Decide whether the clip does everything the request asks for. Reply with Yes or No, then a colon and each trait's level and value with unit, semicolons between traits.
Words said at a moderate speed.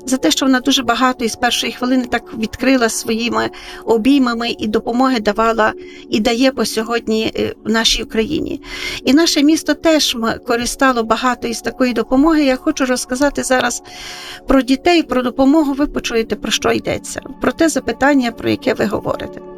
No: fast, 160 wpm